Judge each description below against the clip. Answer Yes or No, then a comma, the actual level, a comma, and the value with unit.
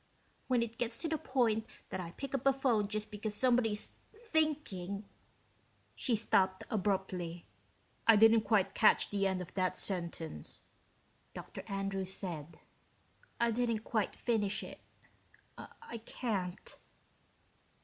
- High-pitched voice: Yes, high, 215 Hz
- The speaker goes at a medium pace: No, slow, 130 wpm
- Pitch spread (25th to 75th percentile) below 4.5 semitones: Yes, average, 3.8 semitones